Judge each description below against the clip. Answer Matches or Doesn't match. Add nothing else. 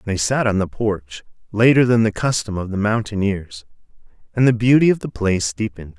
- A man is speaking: Matches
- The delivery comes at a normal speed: Matches